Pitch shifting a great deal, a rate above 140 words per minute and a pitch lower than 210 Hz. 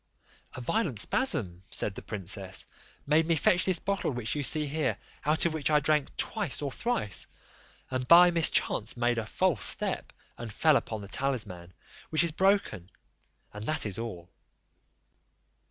Yes: wide, 7.3 semitones; average, 160 wpm; medium, 140 Hz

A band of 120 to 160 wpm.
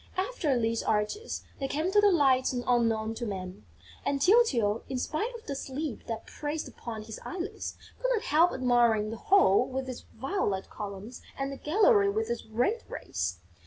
No: average, 175 wpm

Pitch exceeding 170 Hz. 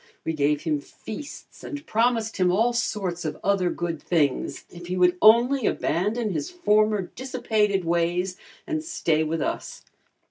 Yes: high, 190 Hz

